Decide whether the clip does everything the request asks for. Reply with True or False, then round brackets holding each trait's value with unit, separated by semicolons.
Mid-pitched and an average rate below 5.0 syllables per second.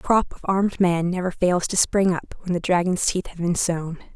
False (180 Hz; 5.2 syllables/s)